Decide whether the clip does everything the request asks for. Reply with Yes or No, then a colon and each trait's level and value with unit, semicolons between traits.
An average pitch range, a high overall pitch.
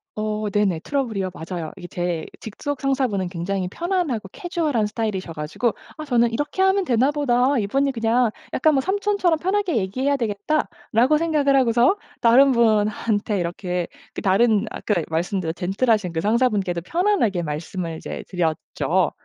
No: wide, 6.7 semitones; high, 225 Hz